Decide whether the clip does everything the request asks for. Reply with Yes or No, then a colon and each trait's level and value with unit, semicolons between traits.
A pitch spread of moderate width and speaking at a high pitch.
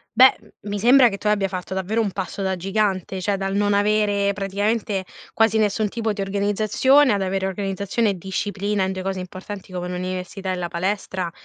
No: narrow, 1.7 semitones; high, 200 Hz